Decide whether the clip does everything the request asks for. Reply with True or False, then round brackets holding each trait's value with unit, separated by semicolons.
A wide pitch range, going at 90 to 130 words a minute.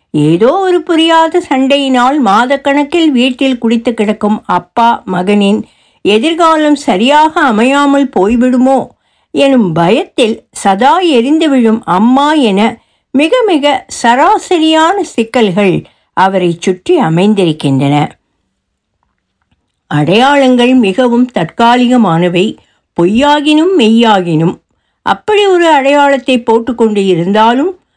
False (6.1 semitones; 80 wpm)